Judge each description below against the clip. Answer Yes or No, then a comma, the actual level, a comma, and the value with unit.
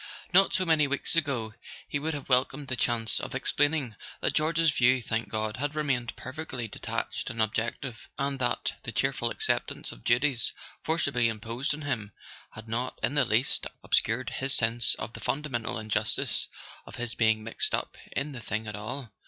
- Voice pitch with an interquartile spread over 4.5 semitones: No, average, 4.2 semitones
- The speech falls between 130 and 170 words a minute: No, average, 185 wpm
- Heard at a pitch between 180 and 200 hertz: No, low, 125 Hz